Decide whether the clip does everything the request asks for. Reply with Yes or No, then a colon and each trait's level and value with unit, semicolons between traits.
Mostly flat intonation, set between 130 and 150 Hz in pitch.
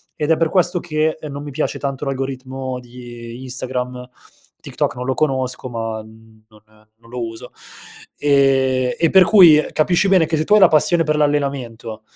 No: average, 3.8 semitones; low, 135 Hz